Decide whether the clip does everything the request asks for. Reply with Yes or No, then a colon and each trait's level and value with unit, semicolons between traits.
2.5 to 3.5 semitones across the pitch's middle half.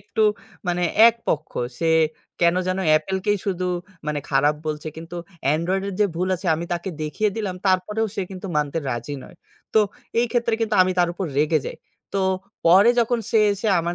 No: average, 3.9 semitones